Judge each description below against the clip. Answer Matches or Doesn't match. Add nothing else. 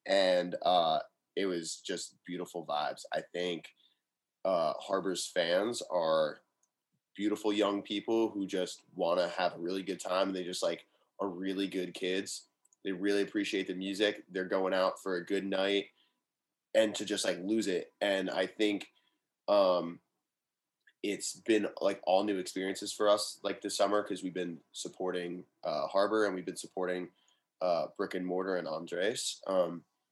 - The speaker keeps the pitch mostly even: Matches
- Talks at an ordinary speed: Matches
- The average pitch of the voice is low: Matches